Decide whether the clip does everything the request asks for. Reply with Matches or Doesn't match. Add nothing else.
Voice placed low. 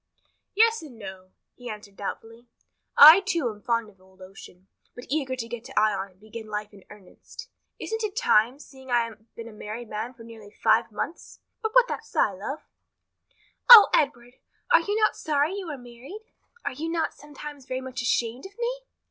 Doesn't match